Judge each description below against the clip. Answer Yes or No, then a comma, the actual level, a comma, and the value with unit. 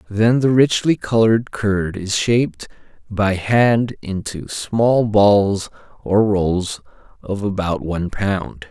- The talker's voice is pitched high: No, low, 100 Hz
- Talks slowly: Yes, slow, 125 wpm